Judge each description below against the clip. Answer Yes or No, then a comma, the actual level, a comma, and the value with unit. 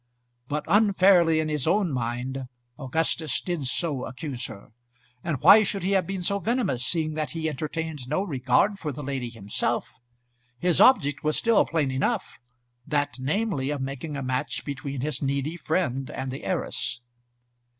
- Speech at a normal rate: Yes, average, 160 wpm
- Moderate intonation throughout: Yes, average, 4.7 semitones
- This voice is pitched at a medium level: Yes, medium, 150 Hz